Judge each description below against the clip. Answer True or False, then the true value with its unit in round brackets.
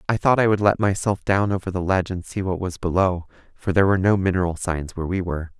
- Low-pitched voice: True (95 Hz)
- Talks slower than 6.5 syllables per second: False (6.6 syllables/s)